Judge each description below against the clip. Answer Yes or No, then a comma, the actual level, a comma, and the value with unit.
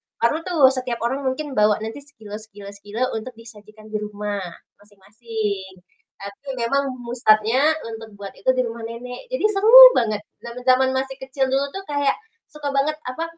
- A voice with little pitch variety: No, average, 4.3 semitones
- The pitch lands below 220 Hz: No, high, 240 Hz